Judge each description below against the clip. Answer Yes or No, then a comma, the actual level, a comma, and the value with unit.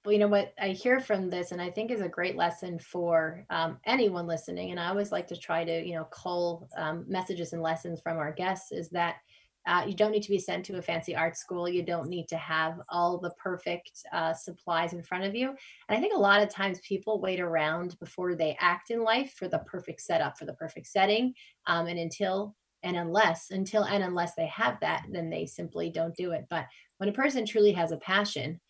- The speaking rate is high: Yes, fast, 235 wpm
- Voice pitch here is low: No, medium, 175 Hz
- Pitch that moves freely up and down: No, average, 3.2 semitones